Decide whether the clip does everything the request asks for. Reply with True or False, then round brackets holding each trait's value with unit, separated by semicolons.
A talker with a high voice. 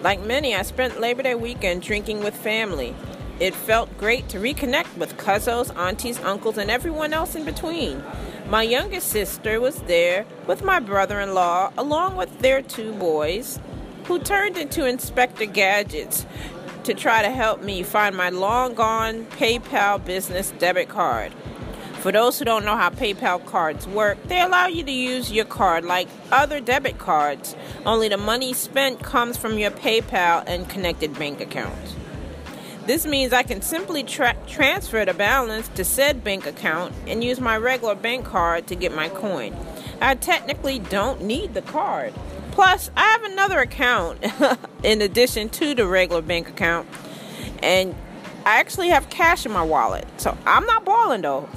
True (225 Hz)